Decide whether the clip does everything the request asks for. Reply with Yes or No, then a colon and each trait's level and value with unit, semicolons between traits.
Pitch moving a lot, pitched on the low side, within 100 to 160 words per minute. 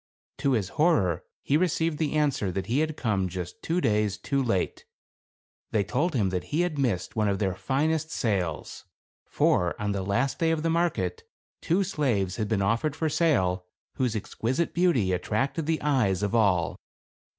No: wide, 8.0 semitones; low, 115 Hz; average, 175 wpm